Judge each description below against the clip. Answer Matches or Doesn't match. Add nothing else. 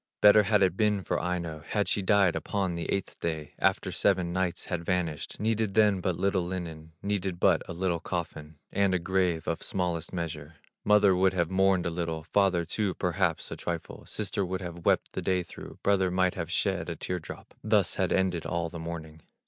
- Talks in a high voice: Doesn't match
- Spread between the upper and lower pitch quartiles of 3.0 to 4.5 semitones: Doesn't match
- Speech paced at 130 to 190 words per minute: Doesn't match